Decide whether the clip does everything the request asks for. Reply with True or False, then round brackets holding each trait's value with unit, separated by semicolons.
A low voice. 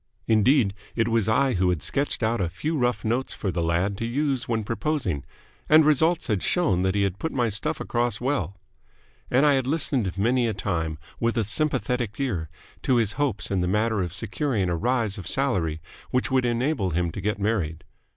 True (115 Hz)